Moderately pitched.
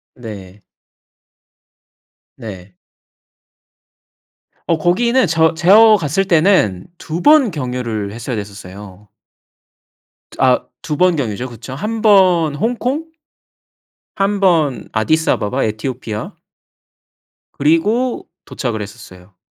Yes: medium, 145 Hz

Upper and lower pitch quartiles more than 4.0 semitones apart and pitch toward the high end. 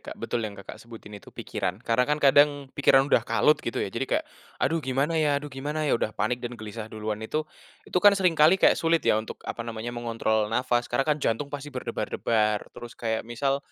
No: average, 4.6 semitones; low, 125 Hz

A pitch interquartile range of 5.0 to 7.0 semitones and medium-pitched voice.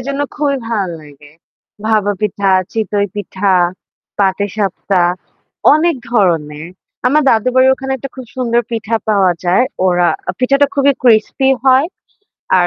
No: wide, 5.5 semitones; high, 215 Hz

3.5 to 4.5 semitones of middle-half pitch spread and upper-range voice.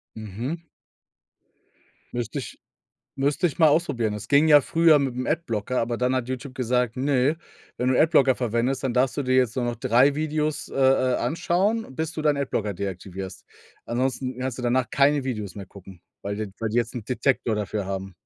No: average, 3.9 semitones; low, 130 Hz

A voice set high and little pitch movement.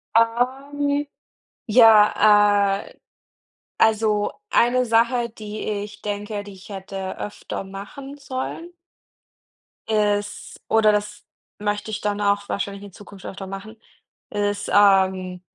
Yes: high, 210 Hz; narrow, 2.1 semitones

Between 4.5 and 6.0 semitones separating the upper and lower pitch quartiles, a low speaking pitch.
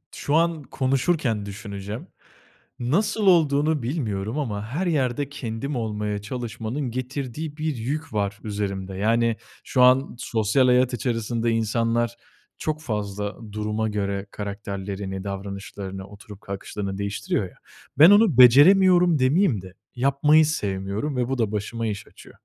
Yes: wide, 5.4 semitones; low, 115 Hz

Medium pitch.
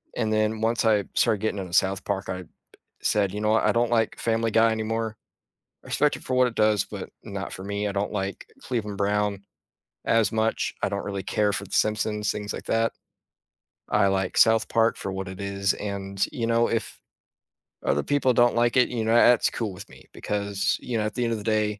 No: low, 105 Hz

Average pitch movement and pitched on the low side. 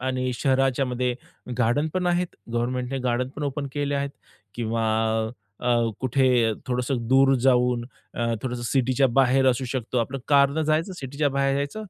No: narrow, 2.3 semitones; low, 130 Hz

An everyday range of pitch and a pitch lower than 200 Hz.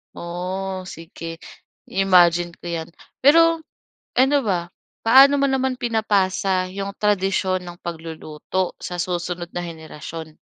Yes: average, 3.3 semitones; medium, 185 Hz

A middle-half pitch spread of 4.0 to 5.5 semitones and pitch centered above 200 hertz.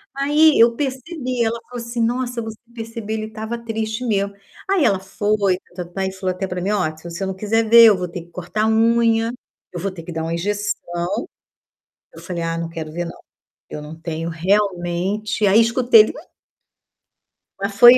Yes: average, 4.5 semitones; high, 210 Hz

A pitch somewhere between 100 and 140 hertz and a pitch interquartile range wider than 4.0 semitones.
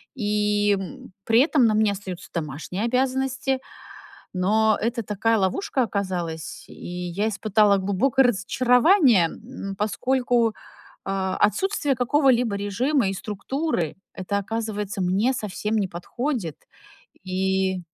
No: high, 210 Hz; average, 4.6 semitones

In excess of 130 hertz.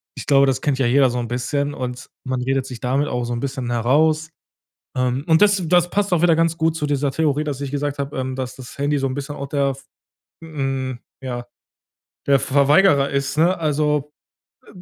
Yes: medium, 140 Hz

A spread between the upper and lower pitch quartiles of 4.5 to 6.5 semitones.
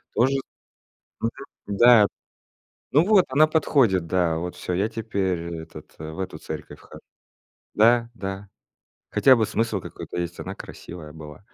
Yes: wide, 5.4 semitones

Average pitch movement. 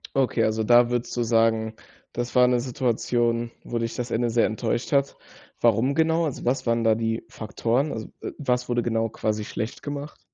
No: narrow, 1.7 semitones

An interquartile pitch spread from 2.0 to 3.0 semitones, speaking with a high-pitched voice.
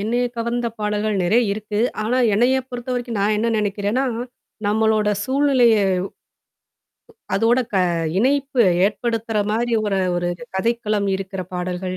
Yes: average, 2.7 semitones; high, 220 Hz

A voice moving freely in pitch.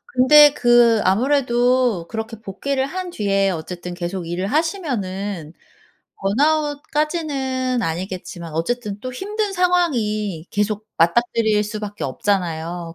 Yes: wide, 6.6 semitones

